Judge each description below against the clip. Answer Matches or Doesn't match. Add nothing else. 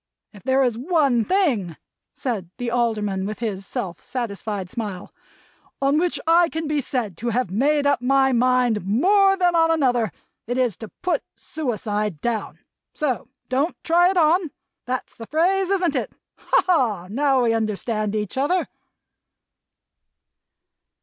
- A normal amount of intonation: Doesn't match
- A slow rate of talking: Doesn't match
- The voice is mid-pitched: Doesn't match